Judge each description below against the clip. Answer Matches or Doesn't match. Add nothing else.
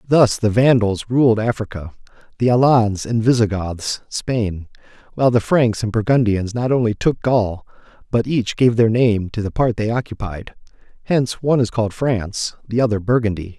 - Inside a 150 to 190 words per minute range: Matches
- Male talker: Matches